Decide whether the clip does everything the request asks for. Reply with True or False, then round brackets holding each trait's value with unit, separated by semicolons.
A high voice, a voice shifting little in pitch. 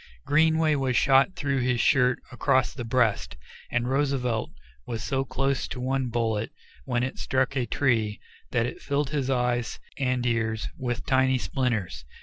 False (125 Hz; 2.2 semitones)